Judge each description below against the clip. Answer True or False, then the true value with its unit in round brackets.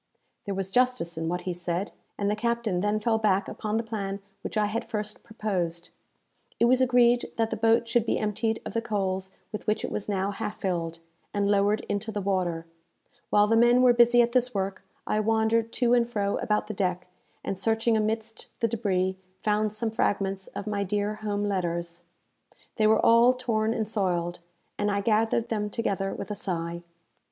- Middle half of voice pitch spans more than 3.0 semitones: False (2.7 semitones)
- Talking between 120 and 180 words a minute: False (195 wpm)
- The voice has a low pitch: False (210 Hz)